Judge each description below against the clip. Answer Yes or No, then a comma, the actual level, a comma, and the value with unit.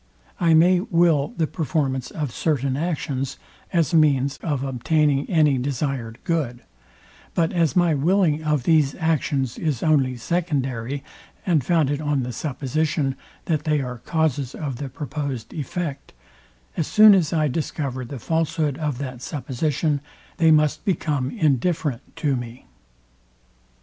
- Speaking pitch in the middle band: Yes, medium, 145 Hz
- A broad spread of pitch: No, average, 3.3 semitones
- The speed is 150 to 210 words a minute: No, slow, 135 wpm